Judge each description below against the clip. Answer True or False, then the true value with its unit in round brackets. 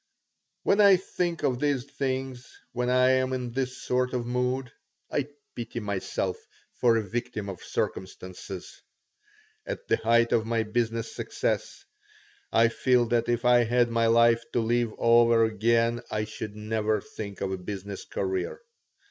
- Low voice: True (120 Hz)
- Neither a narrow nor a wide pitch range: False (2.2 semitones)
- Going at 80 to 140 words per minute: False (155 wpm)